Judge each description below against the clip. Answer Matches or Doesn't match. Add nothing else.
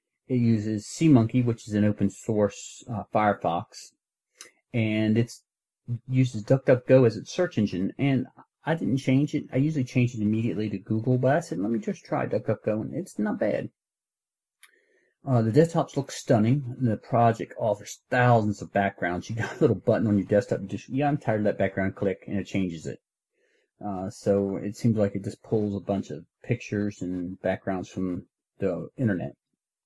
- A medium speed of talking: Matches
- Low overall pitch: Matches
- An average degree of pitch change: Matches